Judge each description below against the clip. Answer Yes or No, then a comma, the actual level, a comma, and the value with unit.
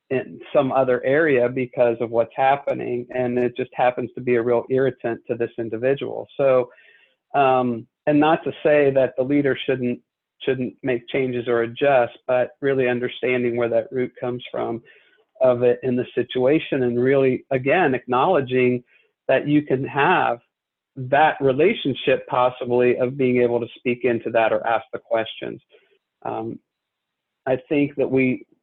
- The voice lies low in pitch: Yes, low, 125 Hz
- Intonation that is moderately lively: No, narrow, 1.7 semitones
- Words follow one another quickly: No, average, 155 wpm